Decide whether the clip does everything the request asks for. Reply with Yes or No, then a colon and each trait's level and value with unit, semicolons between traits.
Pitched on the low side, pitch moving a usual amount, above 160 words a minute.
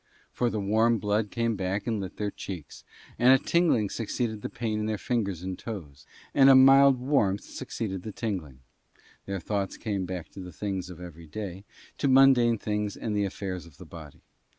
Yes: low, 105 Hz; average, 3.8 semitones; average, 195 wpm